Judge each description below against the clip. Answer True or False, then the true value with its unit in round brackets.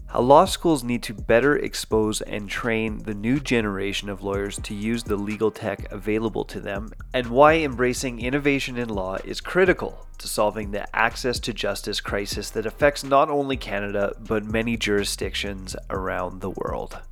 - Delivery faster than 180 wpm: False (170 wpm)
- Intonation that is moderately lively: True (3.4 semitones)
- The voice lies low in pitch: True (110 Hz)